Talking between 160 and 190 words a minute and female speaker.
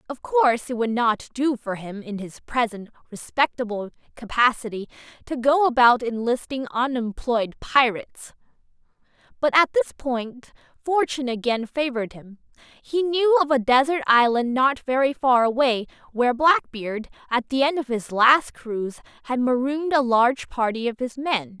No: average, 150 wpm; female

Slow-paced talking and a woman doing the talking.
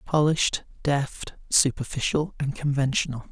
No: slow, 90 wpm; male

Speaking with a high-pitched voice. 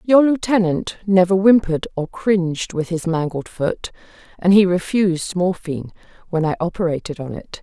No: medium, 180 Hz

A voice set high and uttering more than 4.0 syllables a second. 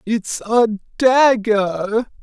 No: high, 225 Hz; 2.3 syllables/s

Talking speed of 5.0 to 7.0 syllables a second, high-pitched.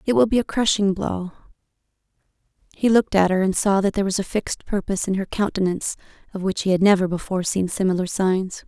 Yes: 6.5 syllables/s; high, 195 Hz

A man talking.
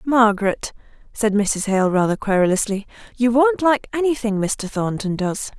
No: female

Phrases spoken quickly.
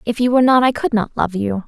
Yes: fast, 320 wpm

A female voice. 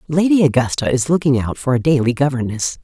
Yes: female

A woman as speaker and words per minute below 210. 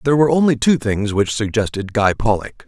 No: male; average, 200 wpm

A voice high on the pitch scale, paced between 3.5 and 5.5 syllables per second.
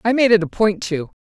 No: high, 205 Hz; 5.7 syllables/s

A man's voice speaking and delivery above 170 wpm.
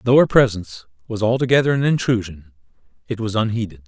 No: male; average, 155 wpm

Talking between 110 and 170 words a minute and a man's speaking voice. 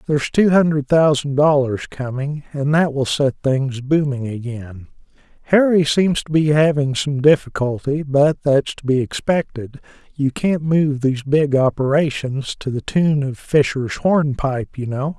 Yes: average, 150 wpm; male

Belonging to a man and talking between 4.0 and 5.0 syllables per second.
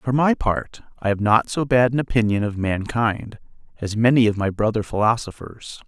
Yes: male; 4.9 syllables/s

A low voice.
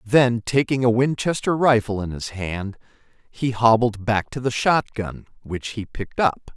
Yes: low, 115 Hz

